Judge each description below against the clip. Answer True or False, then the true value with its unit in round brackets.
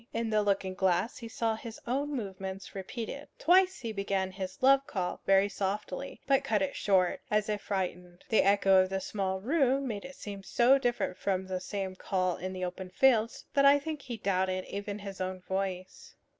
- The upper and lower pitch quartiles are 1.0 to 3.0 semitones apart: False (3.9 semitones)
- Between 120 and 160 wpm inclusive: False (195 wpm)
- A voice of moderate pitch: False (200 Hz)